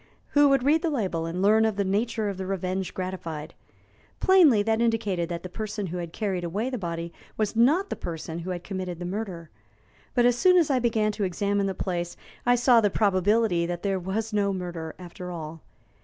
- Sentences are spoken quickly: Yes, fast, 210 wpm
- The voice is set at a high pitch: Yes, high, 195 Hz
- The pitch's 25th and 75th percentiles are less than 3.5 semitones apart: No, average, 4.2 semitones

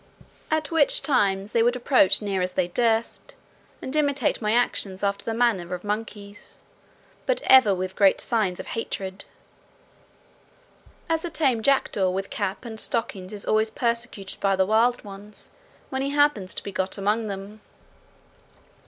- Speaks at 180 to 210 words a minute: No, average, 160 wpm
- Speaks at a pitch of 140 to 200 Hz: No, high, 215 Hz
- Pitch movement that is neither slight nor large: Yes, average, 3.9 semitones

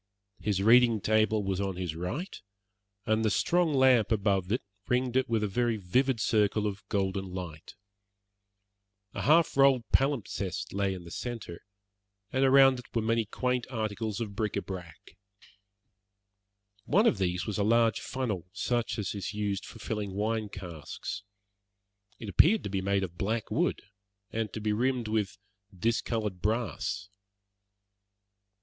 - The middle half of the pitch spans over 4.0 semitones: No, average, 3.5 semitones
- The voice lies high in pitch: No, low, 110 Hz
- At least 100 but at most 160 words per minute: Yes, average, 150 wpm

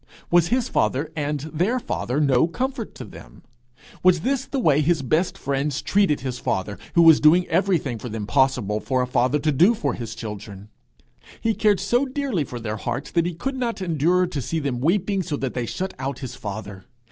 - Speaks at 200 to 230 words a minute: Yes, fast, 205 wpm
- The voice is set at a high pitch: No, medium, 150 Hz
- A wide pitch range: Yes, wide, 6.6 semitones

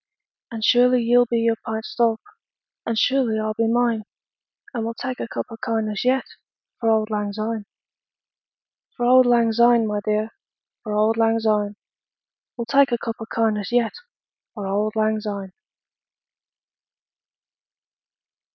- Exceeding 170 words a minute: No, average, 150 wpm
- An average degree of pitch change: No, narrow, 1.7 semitones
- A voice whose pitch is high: Yes, high, 225 Hz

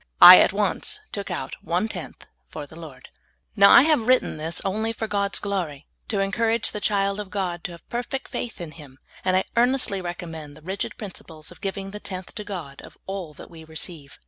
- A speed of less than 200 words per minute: No, fast, 205 wpm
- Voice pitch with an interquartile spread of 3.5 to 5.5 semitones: Yes, average, 4.4 semitones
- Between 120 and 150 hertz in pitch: No, high, 190 Hz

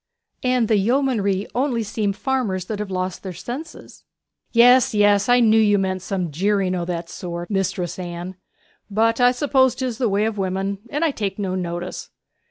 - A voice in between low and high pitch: No, high, 205 Hz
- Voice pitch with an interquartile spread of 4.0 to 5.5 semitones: Yes, average, 4.5 semitones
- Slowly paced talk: No, average, 180 wpm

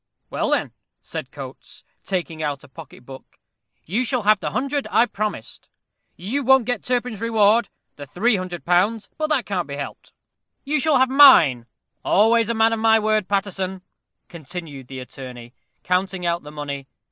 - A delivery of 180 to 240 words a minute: No, average, 170 wpm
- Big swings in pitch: Yes, wide, 6.7 semitones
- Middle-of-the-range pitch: No, high, 195 Hz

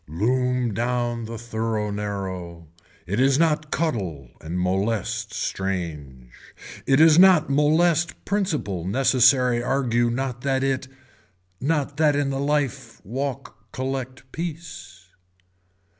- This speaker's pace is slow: Yes, slow, 110 wpm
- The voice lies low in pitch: Yes, low, 125 Hz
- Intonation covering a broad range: Yes, wide, 5.8 semitones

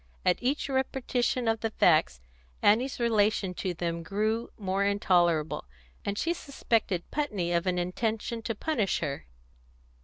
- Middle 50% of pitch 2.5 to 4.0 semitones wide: No, average, 4.8 semitones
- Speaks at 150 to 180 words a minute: No, average, 140 wpm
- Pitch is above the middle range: Yes, high, 210 Hz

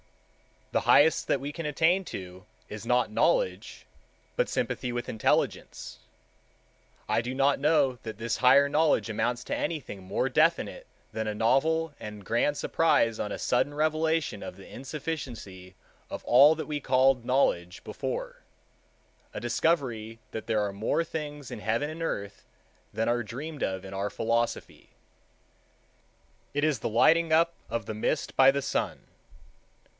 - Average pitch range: No, wide, 5.9 semitones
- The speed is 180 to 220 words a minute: No, average, 150 wpm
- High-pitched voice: No, low, 130 Hz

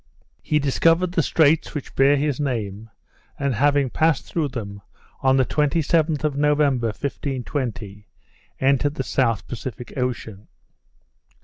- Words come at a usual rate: No, slow, 125 wpm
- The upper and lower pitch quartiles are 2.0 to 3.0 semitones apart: No, average, 3.5 semitones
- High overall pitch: No, low, 135 Hz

